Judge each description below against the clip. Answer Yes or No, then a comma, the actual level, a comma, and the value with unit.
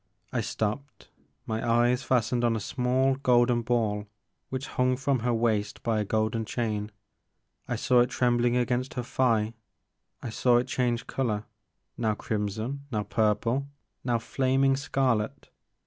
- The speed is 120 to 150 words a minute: Yes, average, 145 wpm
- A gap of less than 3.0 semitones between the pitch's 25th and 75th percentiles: Yes, narrow, 2.6 semitones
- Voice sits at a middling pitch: No, low, 120 Hz